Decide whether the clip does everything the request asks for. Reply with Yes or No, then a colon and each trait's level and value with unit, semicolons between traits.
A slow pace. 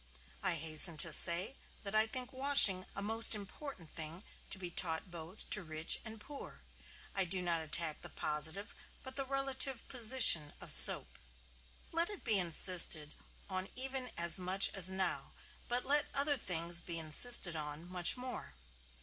No: average, 160 wpm